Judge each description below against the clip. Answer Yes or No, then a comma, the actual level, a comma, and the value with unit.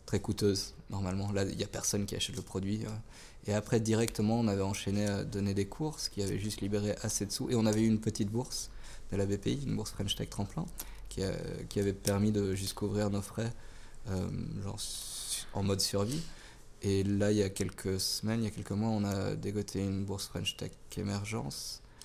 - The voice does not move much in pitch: Yes, narrow, 2.0 semitones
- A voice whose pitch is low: Yes, low, 105 Hz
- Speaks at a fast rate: No, average, 210 wpm